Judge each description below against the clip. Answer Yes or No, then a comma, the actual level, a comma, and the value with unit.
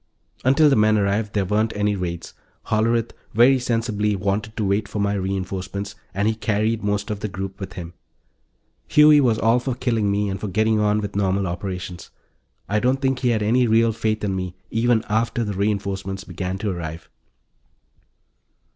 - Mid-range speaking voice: No, low, 105 Hz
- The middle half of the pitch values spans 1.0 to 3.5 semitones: Yes, narrow, 2.6 semitones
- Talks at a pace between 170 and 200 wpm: Yes, average, 175 wpm